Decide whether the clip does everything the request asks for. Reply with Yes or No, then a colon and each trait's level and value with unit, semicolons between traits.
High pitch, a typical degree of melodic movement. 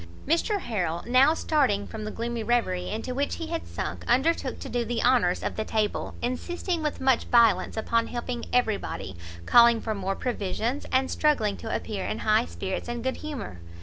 Yes: high, 235 Hz; average, 3.6 semitones